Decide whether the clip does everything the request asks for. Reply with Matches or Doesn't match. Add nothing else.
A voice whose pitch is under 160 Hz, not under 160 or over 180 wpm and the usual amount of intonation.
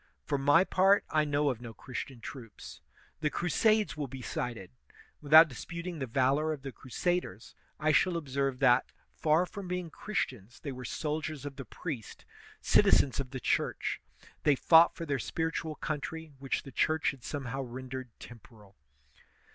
Matches